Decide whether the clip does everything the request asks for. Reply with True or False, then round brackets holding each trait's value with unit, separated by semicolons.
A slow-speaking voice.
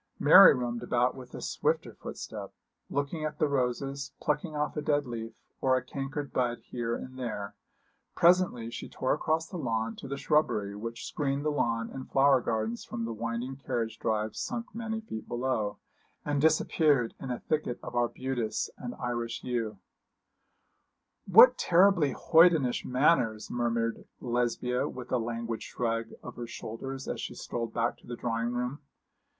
False (160 wpm)